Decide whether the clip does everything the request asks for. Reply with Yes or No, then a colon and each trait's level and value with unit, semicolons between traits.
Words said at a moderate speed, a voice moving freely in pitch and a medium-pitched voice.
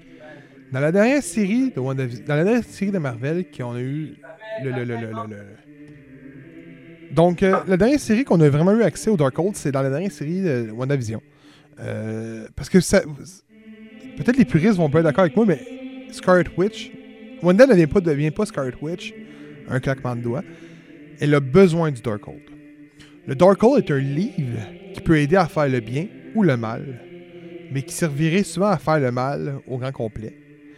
Yes: average, 190 wpm; wide, 6.0 semitones; medium, 155 Hz